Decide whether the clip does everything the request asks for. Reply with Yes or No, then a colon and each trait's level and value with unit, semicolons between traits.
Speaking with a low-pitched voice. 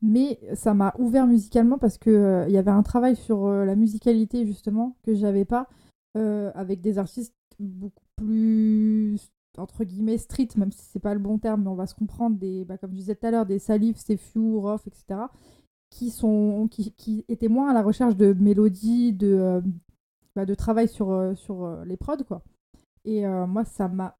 No: high, 215 Hz